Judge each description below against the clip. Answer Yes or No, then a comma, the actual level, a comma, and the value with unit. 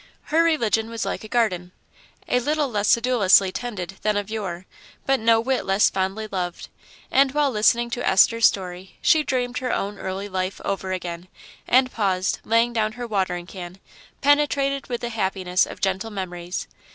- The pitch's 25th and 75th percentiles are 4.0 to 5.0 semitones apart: Yes, average, 4.4 semitones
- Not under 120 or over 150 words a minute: No, average, 170 wpm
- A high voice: Yes, high, 215 Hz